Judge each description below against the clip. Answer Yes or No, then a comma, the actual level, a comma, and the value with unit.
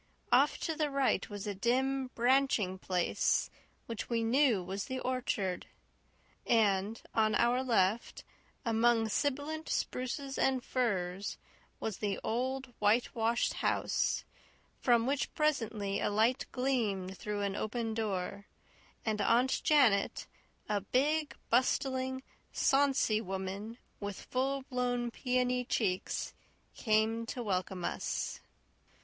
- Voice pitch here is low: No, high, 230 Hz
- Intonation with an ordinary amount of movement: Yes, average, 4.1 semitones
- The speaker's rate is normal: No, slow, 115 wpm